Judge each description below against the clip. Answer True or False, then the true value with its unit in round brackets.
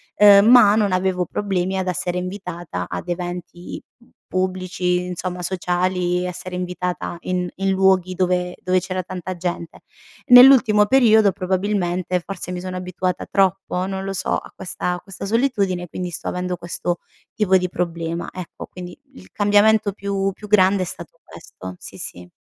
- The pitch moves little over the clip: True (1.6 semitones)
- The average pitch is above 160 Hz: True (185 Hz)